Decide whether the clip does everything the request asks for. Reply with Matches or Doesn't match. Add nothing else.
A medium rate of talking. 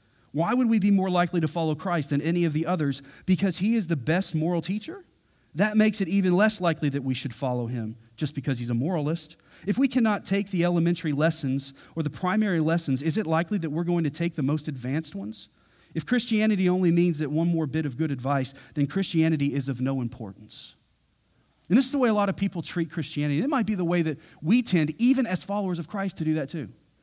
Doesn't match